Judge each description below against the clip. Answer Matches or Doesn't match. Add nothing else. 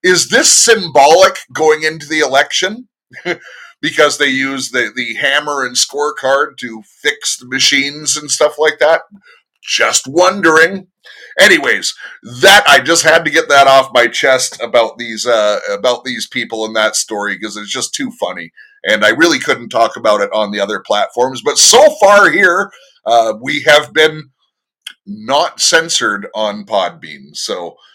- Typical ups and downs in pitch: Doesn't match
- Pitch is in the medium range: Matches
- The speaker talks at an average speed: Matches